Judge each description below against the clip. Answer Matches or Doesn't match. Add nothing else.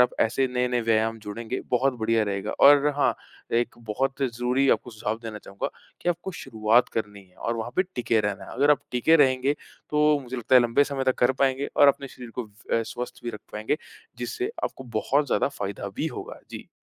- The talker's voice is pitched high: Doesn't match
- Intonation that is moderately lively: Matches